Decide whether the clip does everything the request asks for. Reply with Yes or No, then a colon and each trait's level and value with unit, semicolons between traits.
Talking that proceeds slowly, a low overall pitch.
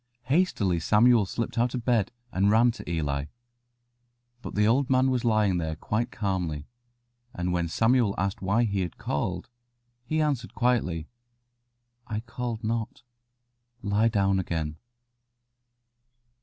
Yes: slow, 130 wpm; low, 105 Hz